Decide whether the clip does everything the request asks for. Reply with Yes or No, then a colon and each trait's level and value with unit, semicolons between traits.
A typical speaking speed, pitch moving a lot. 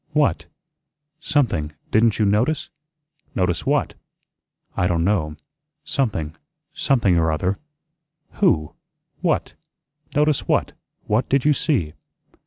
No: slow, 105 wpm; wide, 8.6 semitones